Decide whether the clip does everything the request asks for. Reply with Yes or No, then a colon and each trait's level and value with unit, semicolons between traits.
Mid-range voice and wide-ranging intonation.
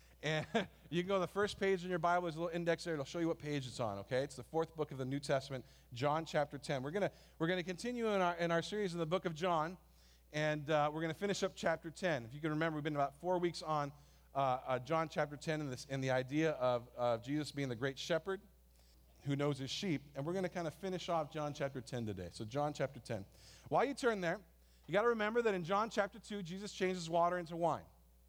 No: medium, 155 Hz; average, 4.6 semitones